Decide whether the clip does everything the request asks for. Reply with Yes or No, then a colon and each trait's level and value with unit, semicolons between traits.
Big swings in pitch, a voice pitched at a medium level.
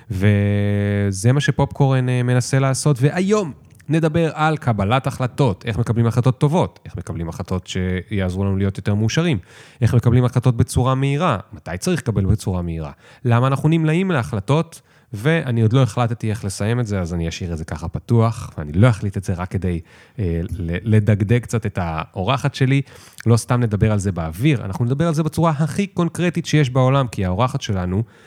No: wide, 5.7 semitones; low, 120 Hz